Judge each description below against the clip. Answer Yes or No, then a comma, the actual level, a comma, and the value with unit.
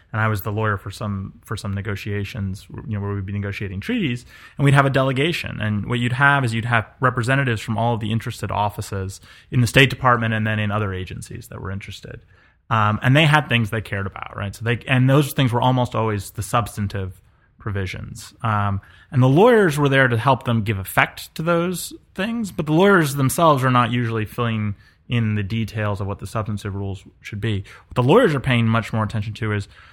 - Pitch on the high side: No, low, 110 Hz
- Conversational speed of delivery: No, fast, 230 wpm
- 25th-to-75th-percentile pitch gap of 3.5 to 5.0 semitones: Yes, average, 3.8 semitones